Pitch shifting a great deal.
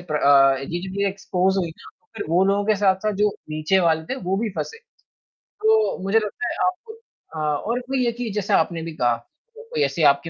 Yes: wide, 6.1 semitones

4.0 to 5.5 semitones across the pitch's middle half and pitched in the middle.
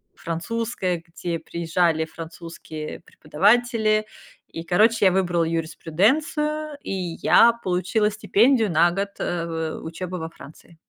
Yes: average, 4.7 semitones; medium, 180 Hz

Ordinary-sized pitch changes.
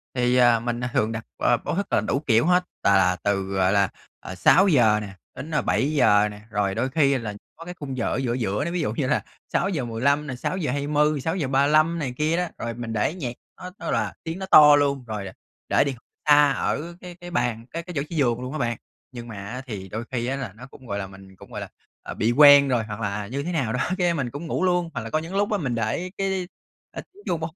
No: wide, 5.8 semitones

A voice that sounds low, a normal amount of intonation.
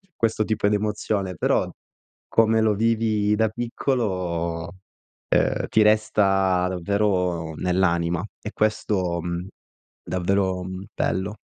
Yes: low, 100 Hz; average, 3.0 semitones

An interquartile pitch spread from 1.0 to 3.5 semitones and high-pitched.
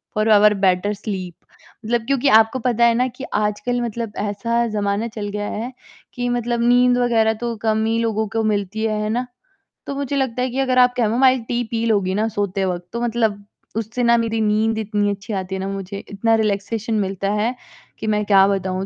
Yes: narrow, 2.6 semitones; high, 220 Hz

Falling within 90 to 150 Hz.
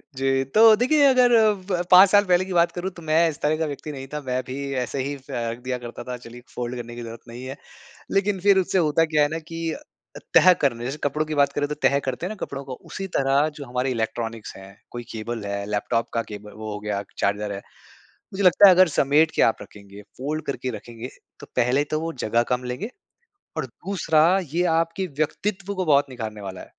Yes: medium, 140 Hz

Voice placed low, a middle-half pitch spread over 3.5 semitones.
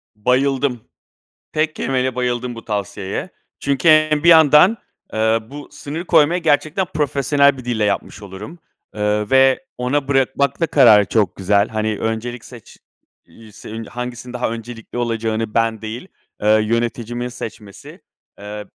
Yes: low, 120 Hz; average, 4.4 semitones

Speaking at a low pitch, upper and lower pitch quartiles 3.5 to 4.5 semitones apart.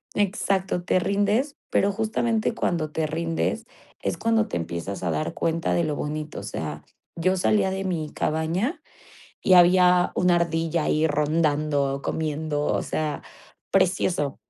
No: medium, 165 Hz; average, 3.8 semitones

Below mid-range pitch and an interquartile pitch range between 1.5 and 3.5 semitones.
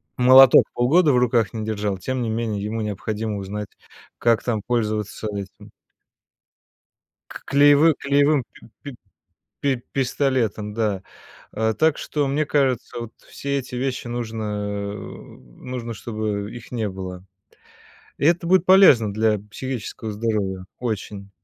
No: low, 115 Hz; average, 3.9 semitones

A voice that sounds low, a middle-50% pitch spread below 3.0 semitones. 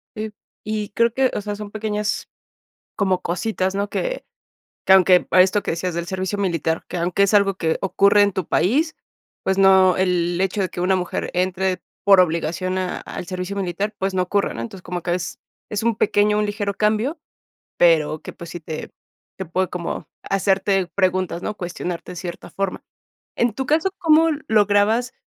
No: high, 190 Hz; narrow, 2.5 semitones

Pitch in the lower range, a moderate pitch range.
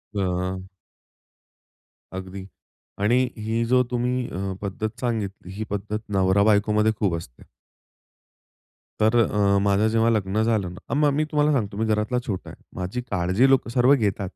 Yes: low, 105 Hz; average, 3.2 semitones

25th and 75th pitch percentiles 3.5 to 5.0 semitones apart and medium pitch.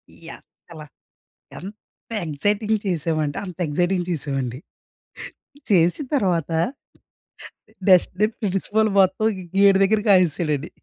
Yes: average, 4.3 semitones; medium, 180 Hz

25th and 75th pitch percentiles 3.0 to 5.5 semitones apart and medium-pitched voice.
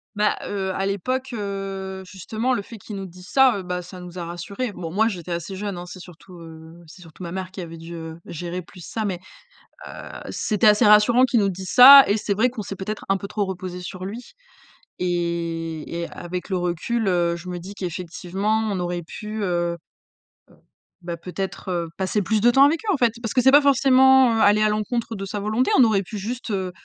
No: average, 3.6 semitones; high, 195 Hz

